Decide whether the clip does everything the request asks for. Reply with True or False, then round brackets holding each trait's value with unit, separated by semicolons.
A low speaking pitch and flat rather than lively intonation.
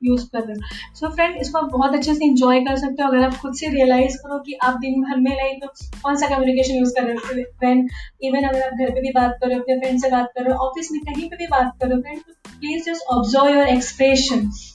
False (260 Hz; 1.9 semitones)